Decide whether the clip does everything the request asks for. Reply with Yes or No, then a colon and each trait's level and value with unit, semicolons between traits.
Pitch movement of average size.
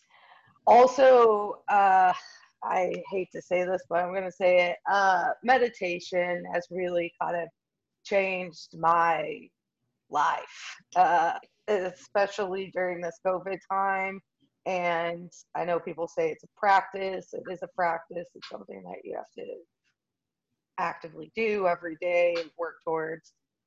No: narrow, 2.2 semitones